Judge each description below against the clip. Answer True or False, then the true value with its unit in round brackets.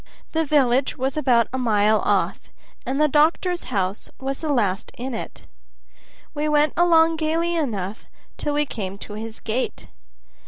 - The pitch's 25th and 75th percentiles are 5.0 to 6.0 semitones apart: True (5.6 semitones)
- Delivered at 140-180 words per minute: True (155 wpm)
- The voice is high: True (265 Hz)